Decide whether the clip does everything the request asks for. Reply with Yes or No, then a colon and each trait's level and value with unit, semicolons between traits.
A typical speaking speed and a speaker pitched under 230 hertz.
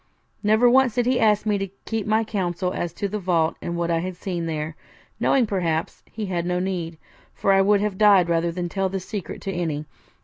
No: fast, 225 wpm; high, 190 Hz